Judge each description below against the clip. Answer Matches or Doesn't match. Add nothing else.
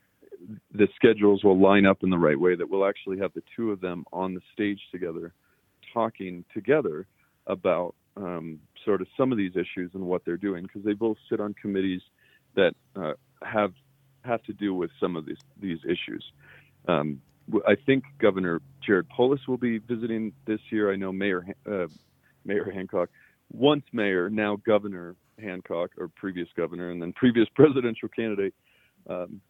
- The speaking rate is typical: Matches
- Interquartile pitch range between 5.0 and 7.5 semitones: Doesn't match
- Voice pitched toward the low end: Matches